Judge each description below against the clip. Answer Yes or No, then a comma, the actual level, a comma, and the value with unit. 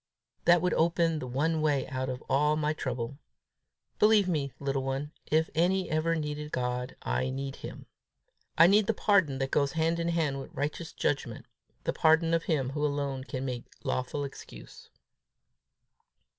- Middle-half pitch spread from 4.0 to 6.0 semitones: No, average, 3.6 semitones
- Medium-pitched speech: Yes, medium, 150 Hz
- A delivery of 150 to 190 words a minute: Yes, average, 165 wpm